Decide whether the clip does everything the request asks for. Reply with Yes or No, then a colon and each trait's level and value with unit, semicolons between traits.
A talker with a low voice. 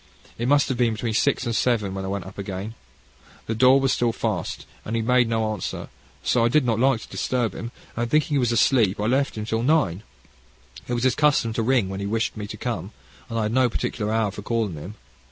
Yes: low, 115 Hz